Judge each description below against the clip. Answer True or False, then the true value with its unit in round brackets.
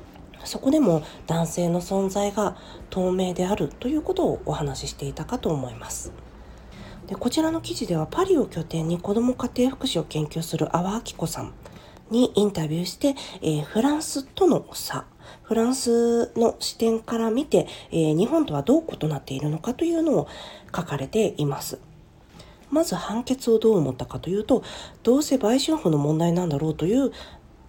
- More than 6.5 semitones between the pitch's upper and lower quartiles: True (8.0 semitones)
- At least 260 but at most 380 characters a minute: True (340 characters per minute)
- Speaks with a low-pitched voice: False (195 Hz)